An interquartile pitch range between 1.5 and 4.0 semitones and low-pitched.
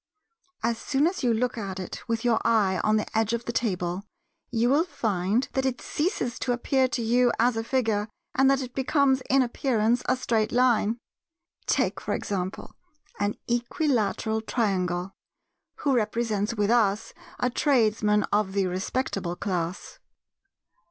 No: average, 3.5 semitones; high, 230 Hz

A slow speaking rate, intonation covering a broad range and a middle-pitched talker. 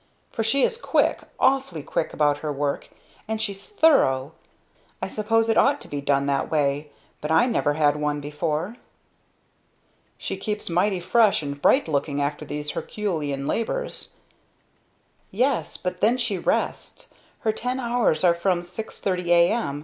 No: average, 155 wpm; wide, 7.4 semitones; medium, 175 Hz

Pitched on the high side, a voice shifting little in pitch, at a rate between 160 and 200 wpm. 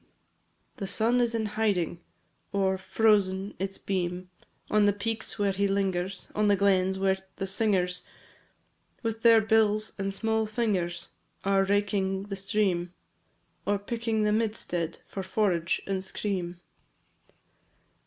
No: high, 200 Hz; narrow, 2.1 semitones; slow, 135 wpm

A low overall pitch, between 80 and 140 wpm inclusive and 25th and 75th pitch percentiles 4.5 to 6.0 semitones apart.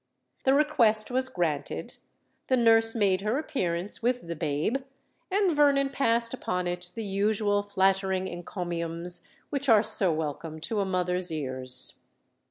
No: high, 200 Hz; slow, 135 wpm; average, 5.2 semitones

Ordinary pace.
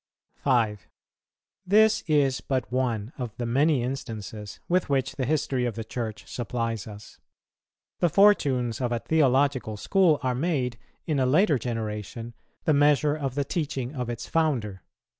Yes: average, 150 wpm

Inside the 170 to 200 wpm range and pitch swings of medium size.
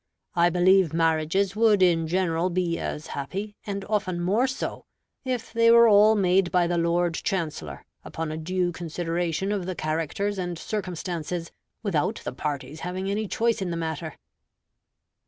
No: average, 155 wpm; average, 3.3 semitones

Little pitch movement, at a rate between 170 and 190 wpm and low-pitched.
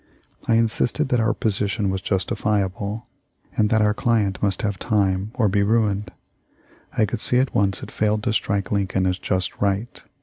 Yes: narrow, 2.2 semitones; average, 175 wpm; low, 105 Hz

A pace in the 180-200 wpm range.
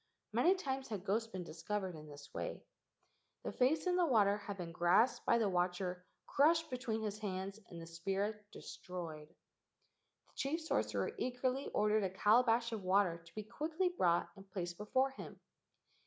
No: average, 170 wpm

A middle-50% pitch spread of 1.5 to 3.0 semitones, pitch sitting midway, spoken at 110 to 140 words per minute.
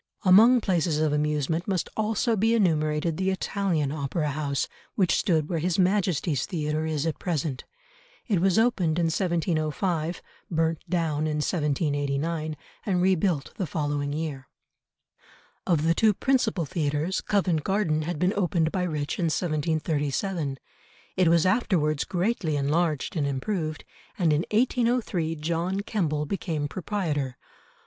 No: average, 3.7 semitones; medium, 165 Hz; slow, 135 wpm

